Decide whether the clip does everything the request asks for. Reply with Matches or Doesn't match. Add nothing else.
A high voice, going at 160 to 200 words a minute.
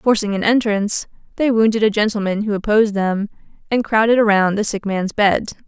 Matches